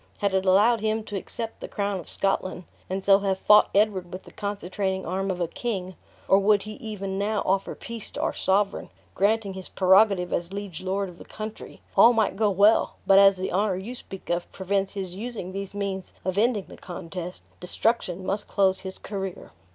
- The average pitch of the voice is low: No, high, 195 Hz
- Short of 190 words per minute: No, average, 200 wpm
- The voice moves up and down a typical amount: No, narrow, 1.8 semitones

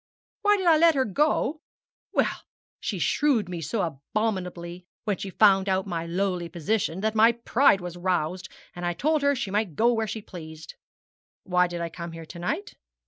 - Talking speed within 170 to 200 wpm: Yes, average, 190 wpm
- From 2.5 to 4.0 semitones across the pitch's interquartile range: No, average, 4.8 semitones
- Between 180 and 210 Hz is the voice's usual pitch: Yes, high, 190 Hz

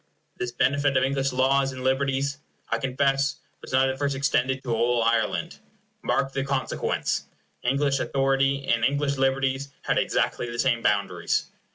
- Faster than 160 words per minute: No, average, 155 wpm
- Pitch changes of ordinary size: No, narrow, 1.4 semitones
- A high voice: No, low, 135 Hz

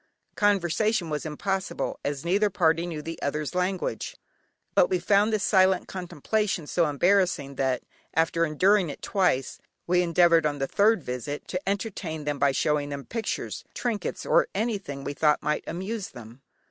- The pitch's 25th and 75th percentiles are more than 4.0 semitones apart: Yes, average, 5.1 semitones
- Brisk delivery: No, average, 160 wpm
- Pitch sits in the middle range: Yes, medium, 170 Hz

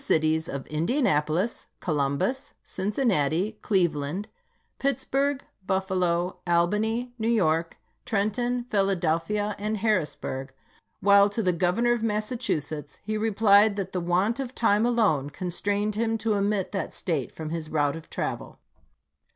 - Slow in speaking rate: Yes, slow, 125 wpm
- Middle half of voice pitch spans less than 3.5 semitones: No, average, 5.0 semitones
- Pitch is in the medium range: No, high, 200 Hz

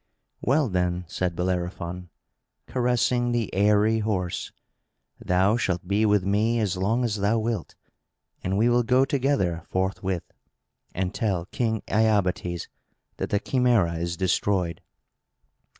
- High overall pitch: No, low, 100 Hz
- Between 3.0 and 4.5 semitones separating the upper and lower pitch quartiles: Yes, average, 4.1 semitones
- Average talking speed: No, slow, 125 wpm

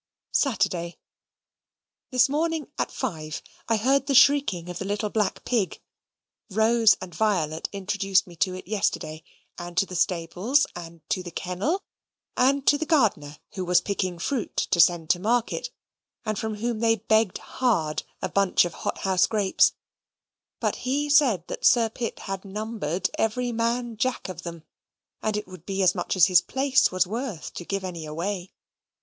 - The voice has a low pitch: No, high, 200 Hz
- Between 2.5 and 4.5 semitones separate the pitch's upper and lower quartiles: No, average, 4.9 semitones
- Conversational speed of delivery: Yes, average, 170 wpm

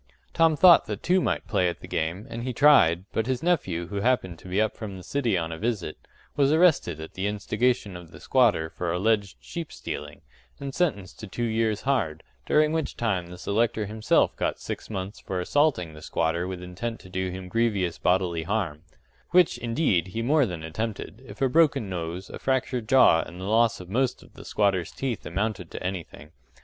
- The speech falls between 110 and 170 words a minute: No, fast, 205 wpm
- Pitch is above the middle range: No, low, 105 Hz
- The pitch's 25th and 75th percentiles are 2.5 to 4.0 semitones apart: No, wide, 5.5 semitones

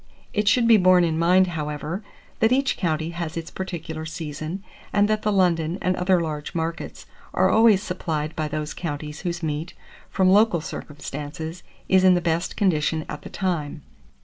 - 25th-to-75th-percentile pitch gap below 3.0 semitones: No, average, 3.3 semitones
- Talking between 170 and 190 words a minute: Yes, average, 175 wpm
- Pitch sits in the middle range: Yes, medium, 170 Hz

